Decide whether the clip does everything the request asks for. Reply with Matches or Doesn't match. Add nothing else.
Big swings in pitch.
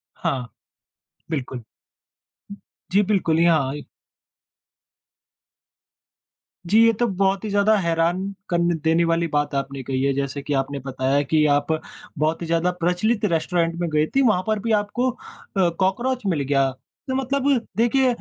Matches